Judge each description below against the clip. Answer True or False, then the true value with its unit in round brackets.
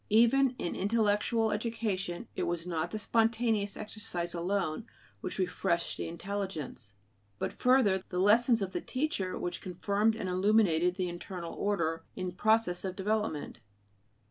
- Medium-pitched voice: False (200 Hz)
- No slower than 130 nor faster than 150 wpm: True (140 wpm)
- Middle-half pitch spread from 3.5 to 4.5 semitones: True (3.8 semitones)